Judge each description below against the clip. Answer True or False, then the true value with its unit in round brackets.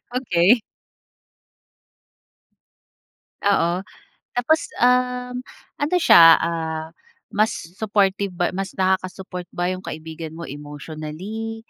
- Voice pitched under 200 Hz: True (185 Hz)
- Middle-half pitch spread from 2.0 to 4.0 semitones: False (5.1 semitones)